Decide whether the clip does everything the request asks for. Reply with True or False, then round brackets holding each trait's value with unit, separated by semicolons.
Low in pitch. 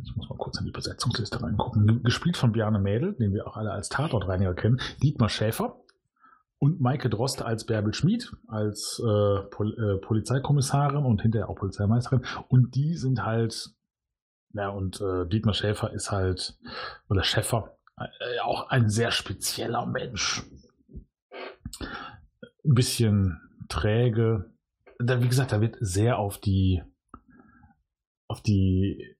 True (110 Hz)